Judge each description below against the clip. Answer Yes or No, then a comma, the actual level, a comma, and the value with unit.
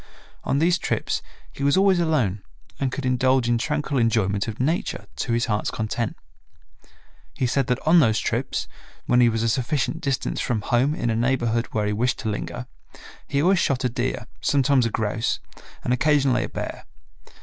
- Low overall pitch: Yes, low, 125 Hz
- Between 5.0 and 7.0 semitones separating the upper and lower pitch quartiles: No, average, 3.5 semitones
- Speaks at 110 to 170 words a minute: No, average, 180 wpm